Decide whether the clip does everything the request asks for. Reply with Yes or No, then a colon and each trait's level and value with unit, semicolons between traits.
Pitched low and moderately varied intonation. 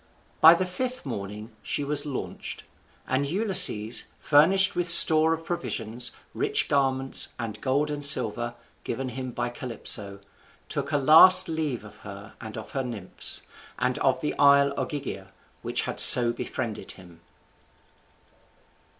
No: low, 130 Hz; wide, 5.8 semitones